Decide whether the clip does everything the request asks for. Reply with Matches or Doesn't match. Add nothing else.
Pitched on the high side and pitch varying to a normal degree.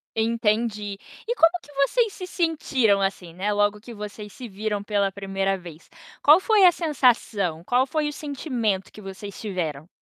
Doesn't match